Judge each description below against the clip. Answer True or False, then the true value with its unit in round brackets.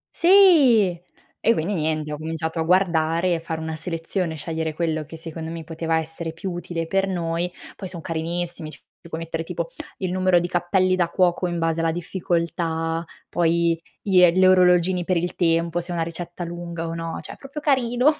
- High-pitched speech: False (170 Hz)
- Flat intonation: True (1.9 semitones)